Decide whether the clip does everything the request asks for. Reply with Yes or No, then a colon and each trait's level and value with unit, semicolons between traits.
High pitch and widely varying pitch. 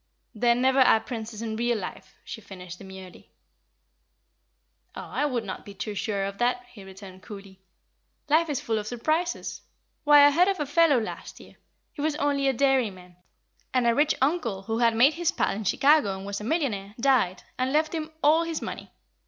Yes: high, 240 Hz; wide, 6.3 semitones